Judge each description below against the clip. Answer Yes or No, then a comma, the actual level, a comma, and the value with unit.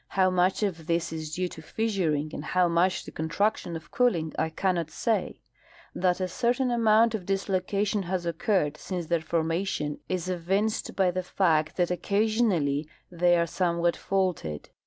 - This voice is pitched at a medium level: Yes, medium, 180 Hz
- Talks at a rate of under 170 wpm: Yes, average, 160 wpm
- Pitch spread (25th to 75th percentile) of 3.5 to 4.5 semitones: No, average, 3.1 semitones